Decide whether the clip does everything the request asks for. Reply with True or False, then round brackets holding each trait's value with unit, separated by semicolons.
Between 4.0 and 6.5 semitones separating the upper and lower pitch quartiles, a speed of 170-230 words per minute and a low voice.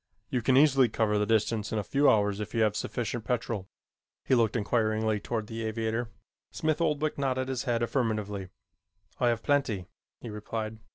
False (2.8 semitones; 175 wpm; 115 Hz)